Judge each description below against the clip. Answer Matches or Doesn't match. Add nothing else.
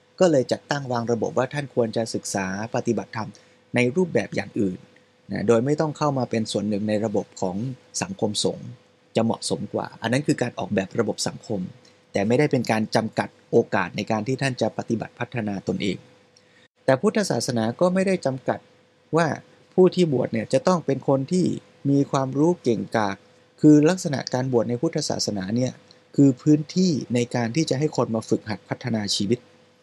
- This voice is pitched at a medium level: Doesn't match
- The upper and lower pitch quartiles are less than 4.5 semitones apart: Doesn't match